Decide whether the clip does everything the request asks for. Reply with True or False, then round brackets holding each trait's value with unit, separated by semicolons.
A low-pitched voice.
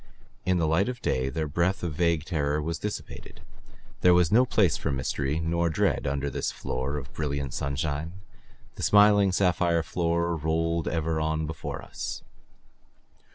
True (80 Hz)